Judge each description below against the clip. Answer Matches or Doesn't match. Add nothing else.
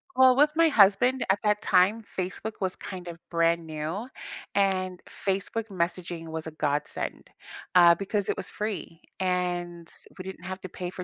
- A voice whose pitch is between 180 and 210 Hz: Matches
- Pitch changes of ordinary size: Matches